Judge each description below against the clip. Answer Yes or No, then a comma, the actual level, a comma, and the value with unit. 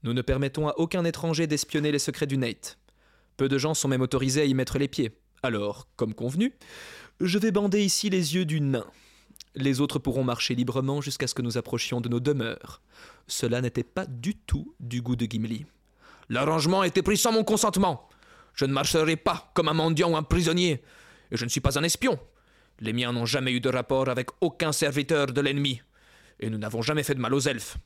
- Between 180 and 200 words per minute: No, average, 215 wpm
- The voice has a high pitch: No, medium, 140 Hz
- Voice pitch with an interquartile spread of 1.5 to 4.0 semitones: No, average, 4.6 semitones